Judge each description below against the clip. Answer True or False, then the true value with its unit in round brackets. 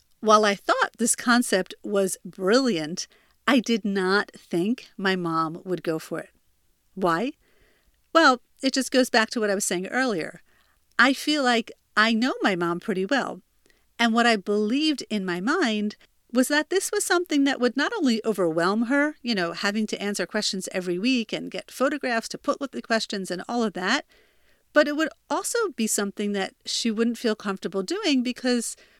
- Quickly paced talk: False (185 wpm)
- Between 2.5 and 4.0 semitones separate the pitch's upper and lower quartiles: False (5.1 semitones)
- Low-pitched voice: False (225 Hz)